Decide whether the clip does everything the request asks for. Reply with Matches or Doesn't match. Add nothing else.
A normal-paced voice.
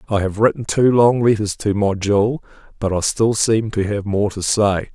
Doesn't match